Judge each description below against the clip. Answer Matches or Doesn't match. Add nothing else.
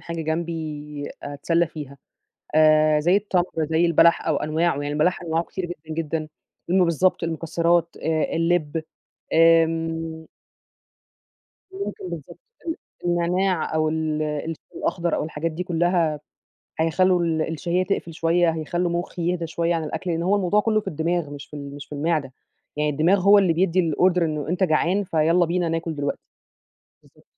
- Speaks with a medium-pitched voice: Matches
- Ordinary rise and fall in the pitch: Doesn't match